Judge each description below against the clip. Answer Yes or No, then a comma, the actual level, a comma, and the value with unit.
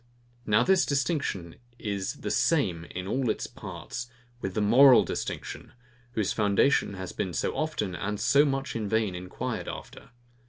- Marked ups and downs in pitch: Yes, wide, 6.2 semitones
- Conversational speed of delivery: Yes, average, 155 wpm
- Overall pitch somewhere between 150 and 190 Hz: No, low, 105 Hz